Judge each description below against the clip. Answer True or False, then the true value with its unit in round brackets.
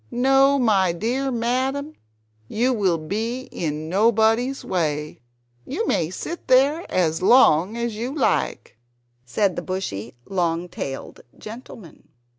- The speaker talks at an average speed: False (120 wpm)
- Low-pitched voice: False (215 Hz)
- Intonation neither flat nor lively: False (7.2 semitones)